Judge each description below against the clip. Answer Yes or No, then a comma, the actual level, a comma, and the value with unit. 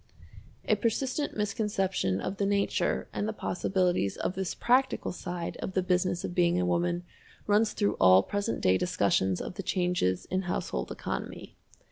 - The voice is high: No, medium, 180 Hz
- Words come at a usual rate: Yes, average, 160 wpm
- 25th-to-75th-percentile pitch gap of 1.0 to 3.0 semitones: Yes, average, 2.7 semitones